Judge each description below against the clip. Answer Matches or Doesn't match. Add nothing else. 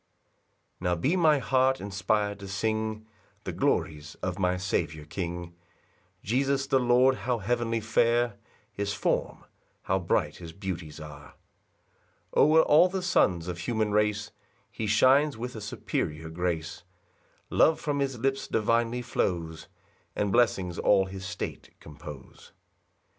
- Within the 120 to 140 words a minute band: Matches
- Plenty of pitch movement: Matches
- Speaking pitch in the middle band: Doesn't match